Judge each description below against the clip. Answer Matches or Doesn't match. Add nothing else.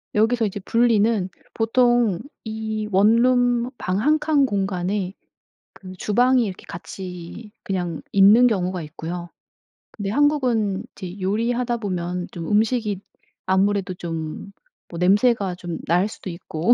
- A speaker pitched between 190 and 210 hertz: Matches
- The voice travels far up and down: Doesn't match